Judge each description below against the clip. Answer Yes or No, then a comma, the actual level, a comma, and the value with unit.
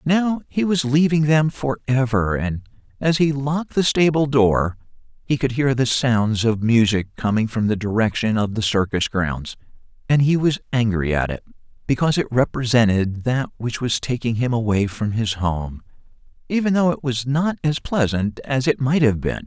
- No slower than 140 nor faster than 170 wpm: No, average, 180 wpm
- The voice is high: No, low, 125 Hz